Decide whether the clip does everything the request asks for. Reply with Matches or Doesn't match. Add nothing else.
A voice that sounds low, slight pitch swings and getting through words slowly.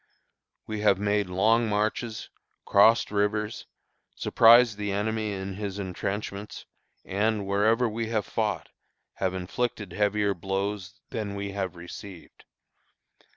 Matches